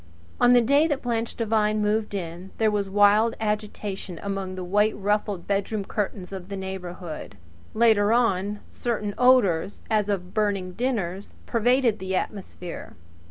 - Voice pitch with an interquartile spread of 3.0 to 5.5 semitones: No, narrow, 2.6 semitones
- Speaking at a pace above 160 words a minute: No, average, 145 wpm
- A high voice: Yes, high, 205 Hz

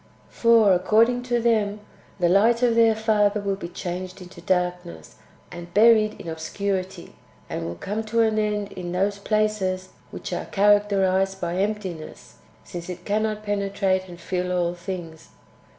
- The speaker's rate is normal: Yes, average, 150 wpm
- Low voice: No, high, 195 Hz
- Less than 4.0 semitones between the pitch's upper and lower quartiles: Yes, average, 2.9 semitones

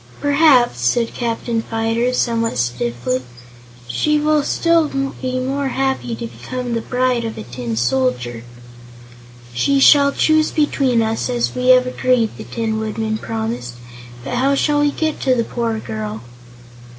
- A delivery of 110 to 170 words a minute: Yes, average, 150 wpm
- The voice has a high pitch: Yes, high, 235 Hz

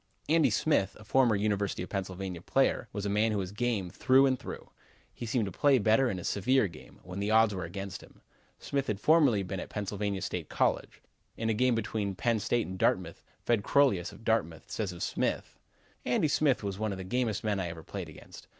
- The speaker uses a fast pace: Yes, fast, 215 wpm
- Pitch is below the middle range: Yes, low, 105 Hz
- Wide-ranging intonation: No, average, 4.1 semitones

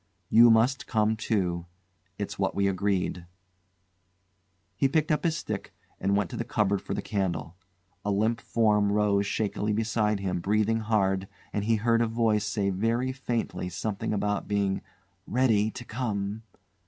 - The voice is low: Yes, low, 105 Hz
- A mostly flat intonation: Yes, narrow, 2.3 semitones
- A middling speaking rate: Yes, average, 155 wpm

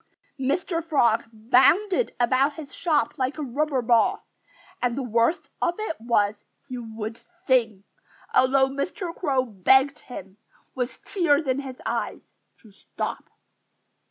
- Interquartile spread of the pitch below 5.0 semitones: Yes, average, 4.3 semitones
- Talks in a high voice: Yes, very high, 260 Hz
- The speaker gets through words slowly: Yes, slow, 130 wpm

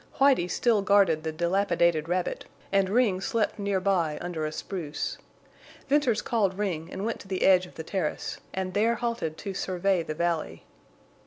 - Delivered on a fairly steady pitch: No, average, 3.3 semitones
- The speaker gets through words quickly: No, average, 170 wpm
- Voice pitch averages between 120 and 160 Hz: No, high, 190 Hz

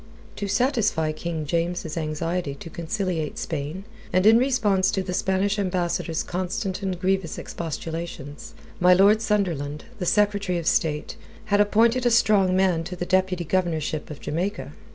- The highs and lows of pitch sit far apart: No, average, 3.5 semitones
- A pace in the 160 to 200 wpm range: No, average, 150 wpm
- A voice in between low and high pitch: Yes, medium, 180 Hz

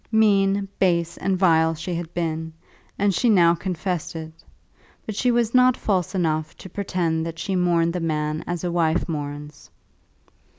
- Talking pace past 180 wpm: No, average, 165 wpm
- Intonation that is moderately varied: Yes, average, 3.3 semitones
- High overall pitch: No, medium, 175 Hz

